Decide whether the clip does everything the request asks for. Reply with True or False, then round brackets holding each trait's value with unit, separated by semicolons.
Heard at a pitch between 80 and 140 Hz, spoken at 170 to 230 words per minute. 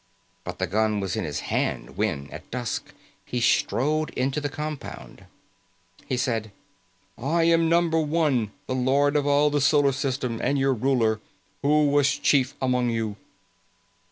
False (135 Hz; 155 wpm)